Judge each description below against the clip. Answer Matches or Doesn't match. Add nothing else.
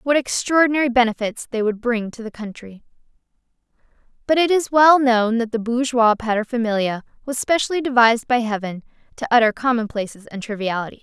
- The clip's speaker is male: Doesn't match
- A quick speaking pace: Doesn't match